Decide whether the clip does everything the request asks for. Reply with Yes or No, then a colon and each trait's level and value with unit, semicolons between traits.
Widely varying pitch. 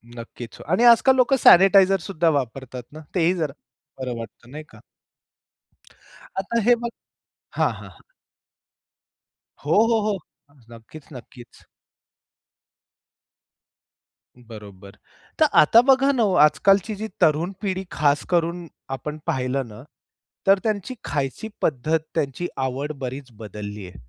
Yes: wide, 7.4 semitones